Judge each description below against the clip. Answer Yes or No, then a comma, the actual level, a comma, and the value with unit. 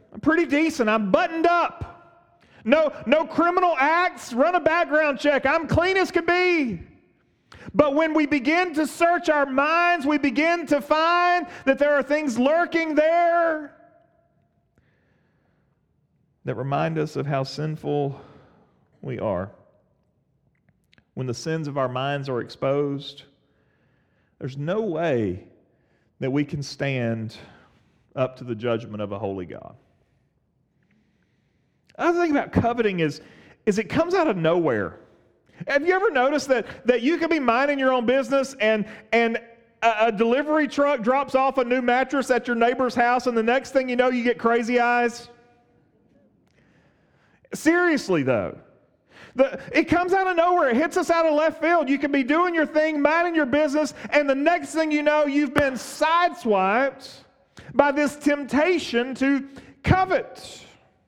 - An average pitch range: No, wide, 5.9 semitones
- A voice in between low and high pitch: No, very high, 275 Hz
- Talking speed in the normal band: Yes, average, 155 wpm